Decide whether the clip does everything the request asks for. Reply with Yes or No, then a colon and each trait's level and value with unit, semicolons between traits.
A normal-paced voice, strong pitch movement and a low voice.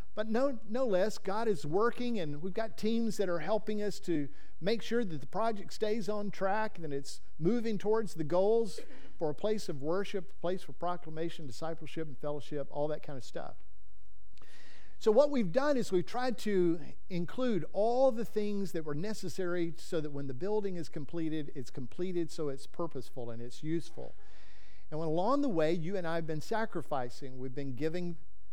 No: average, 195 wpm; wide, 6.1 semitones; medium, 175 Hz